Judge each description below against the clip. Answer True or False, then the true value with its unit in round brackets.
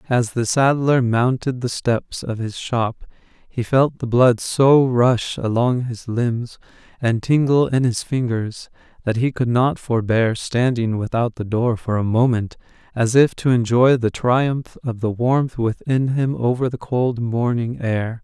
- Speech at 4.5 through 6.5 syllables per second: False (3.9 syllables/s)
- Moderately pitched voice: False (120 Hz)